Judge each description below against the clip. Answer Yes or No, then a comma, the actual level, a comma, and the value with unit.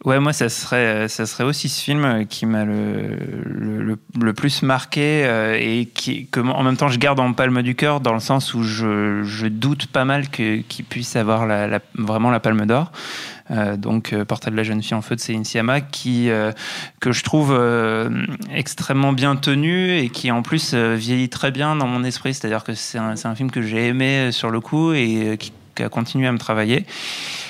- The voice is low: Yes, low, 120 Hz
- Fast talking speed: Yes, fast, 225 wpm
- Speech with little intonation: No, average, 3.6 semitones